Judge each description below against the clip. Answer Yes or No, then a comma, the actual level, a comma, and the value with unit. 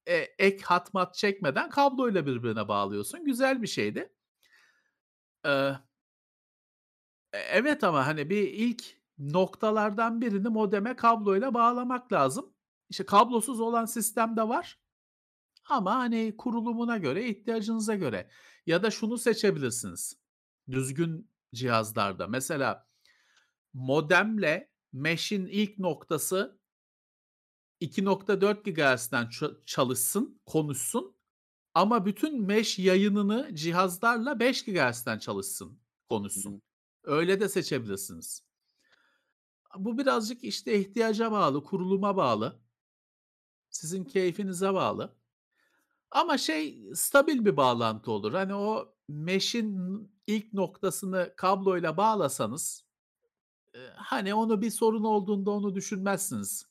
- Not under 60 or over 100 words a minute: Yes, slow, 95 wpm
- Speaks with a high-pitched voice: Yes, high, 200 Hz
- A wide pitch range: Yes, wide, 6.0 semitones